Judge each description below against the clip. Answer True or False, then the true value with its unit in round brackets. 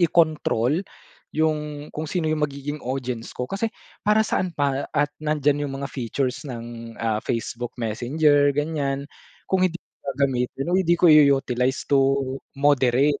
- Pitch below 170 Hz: True (140 Hz)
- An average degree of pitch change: True (3.3 semitones)